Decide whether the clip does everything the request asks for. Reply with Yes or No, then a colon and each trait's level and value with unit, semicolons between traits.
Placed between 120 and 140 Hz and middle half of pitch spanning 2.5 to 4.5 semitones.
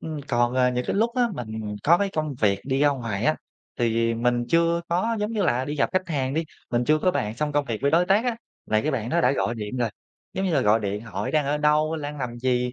No: low, 135 Hz; average, 5.1 semitones